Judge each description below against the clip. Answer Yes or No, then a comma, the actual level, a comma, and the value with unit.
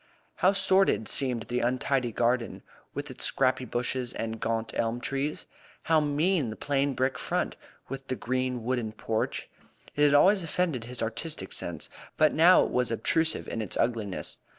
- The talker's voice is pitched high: No, low, 130 Hz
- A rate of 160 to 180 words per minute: Yes, average, 165 wpm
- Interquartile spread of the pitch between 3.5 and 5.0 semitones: Yes, average, 3.9 semitones